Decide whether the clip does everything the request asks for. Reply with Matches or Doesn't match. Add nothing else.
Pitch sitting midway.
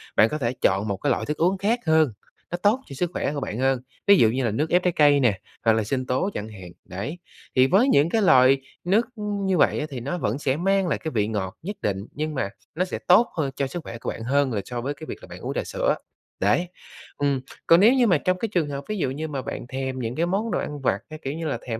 Matches